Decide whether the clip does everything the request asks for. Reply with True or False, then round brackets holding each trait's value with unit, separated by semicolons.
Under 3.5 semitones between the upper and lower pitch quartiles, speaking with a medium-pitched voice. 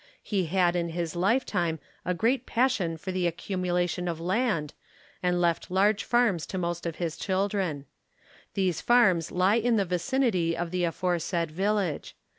True (2.9 semitones; 180 Hz)